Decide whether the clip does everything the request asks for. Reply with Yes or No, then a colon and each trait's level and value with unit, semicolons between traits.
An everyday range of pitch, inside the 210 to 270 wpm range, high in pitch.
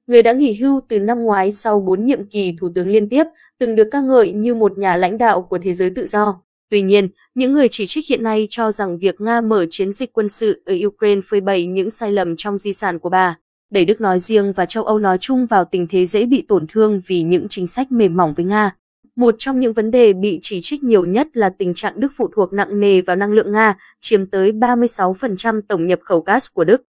Yes: average, 3.6 semitones; fast, 250 wpm; high, 205 Hz